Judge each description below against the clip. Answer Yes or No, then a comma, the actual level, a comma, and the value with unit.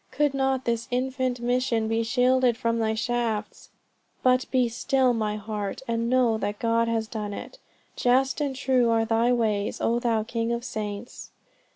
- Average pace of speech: Yes, average, 170 wpm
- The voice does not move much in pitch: Yes, narrow, 2.3 semitones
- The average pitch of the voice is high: Yes, high, 235 Hz